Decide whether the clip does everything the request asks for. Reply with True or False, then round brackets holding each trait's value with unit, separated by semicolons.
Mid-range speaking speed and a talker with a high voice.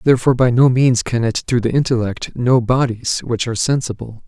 False (195 wpm; 120 Hz)